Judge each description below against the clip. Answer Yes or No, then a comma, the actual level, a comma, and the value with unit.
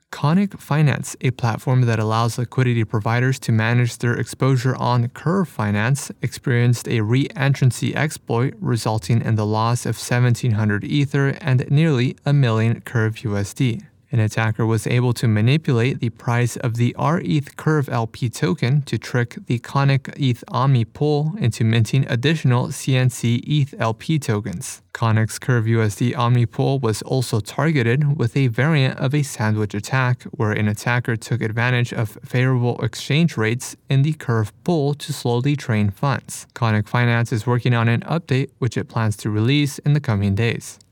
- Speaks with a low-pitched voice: Yes, low, 125 Hz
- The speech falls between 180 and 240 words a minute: No, average, 160 wpm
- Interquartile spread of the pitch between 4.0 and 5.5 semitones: No, average, 3.4 semitones